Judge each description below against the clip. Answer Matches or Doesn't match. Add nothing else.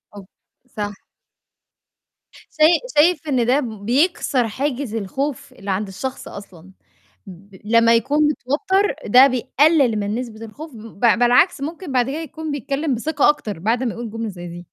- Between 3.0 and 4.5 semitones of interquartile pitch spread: Doesn't match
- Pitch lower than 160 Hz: Doesn't match